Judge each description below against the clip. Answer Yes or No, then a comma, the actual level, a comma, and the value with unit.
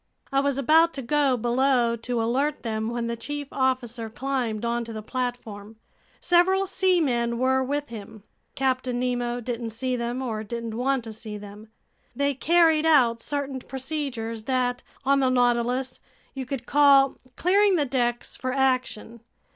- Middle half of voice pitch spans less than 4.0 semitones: Yes, average, 2.8 semitones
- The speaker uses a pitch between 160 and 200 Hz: No, very high, 255 Hz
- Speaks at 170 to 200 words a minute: No, average, 155 wpm